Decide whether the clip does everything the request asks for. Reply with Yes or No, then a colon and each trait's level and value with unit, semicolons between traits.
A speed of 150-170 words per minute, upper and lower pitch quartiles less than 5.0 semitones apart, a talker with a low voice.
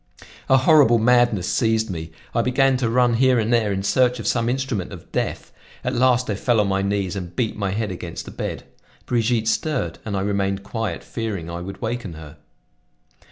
No: average, 200 wpm; average, 4.0 semitones; low, 110 Hz